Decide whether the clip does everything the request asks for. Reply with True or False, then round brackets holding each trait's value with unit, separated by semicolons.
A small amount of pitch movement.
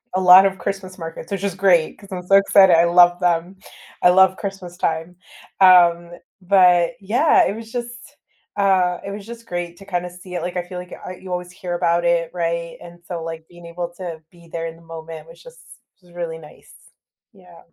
True (2.0 semitones)